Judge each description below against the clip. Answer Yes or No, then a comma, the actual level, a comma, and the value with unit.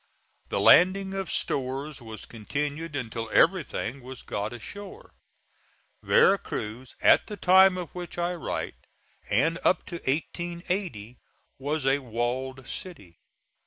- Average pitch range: No, wide, 6.5 semitones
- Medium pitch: Yes, medium, 145 Hz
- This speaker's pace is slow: Yes, slow, 125 wpm